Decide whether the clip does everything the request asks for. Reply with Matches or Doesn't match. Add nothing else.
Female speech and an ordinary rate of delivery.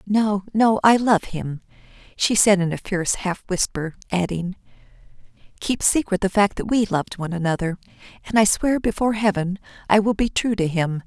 Matches